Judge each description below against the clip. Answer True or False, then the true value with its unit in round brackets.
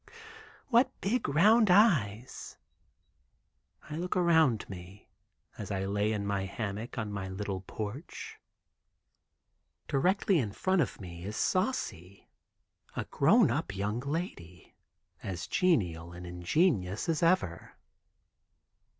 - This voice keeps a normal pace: False (125 wpm)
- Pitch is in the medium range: False (105 Hz)